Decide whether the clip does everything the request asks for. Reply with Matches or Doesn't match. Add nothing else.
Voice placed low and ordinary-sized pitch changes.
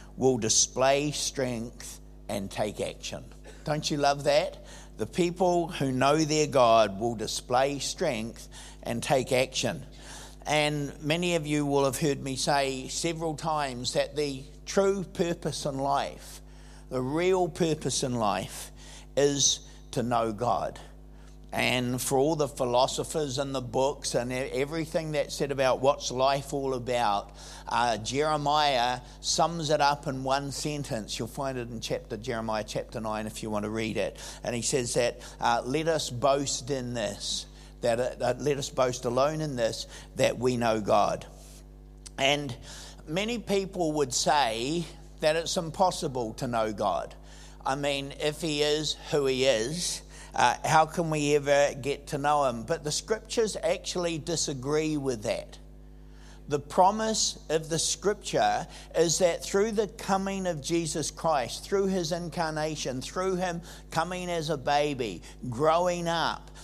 Doesn't match